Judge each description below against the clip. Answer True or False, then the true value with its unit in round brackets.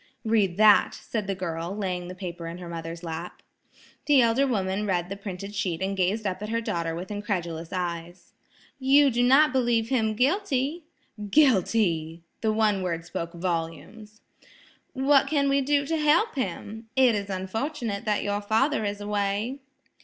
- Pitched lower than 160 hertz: False (205 Hz)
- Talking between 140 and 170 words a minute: True (165 wpm)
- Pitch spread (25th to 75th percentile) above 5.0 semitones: True (5.6 semitones)